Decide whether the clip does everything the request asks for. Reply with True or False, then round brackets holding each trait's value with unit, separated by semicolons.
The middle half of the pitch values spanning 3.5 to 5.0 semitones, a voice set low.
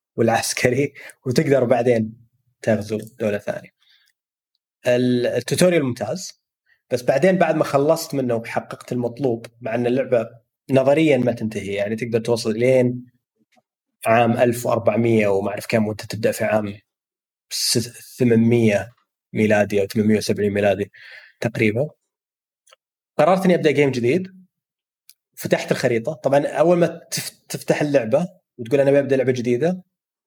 True (4.5 semitones; 125 Hz)